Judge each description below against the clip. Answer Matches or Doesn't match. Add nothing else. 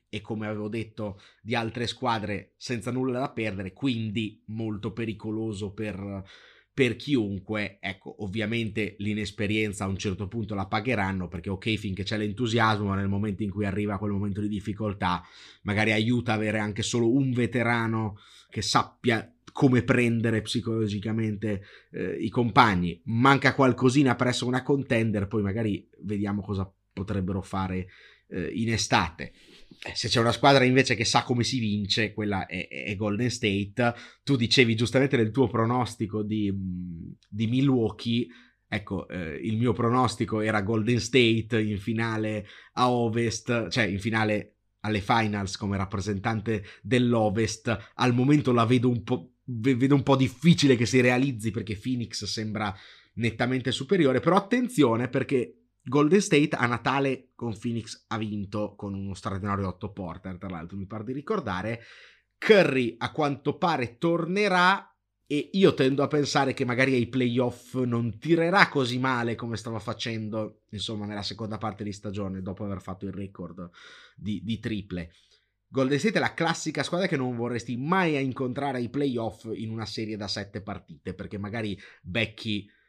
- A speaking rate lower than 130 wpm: Doesn't match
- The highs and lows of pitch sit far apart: Doesn't match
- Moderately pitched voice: Doesn't match